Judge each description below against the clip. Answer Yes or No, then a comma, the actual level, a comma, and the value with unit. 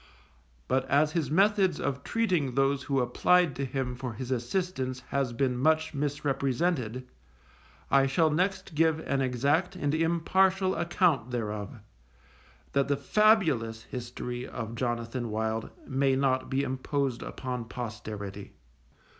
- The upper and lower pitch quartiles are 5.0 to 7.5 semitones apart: No, average, 4.5 semitones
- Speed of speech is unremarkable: No, slow, 130 wpm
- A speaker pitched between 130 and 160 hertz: Yes, low, 135 Hz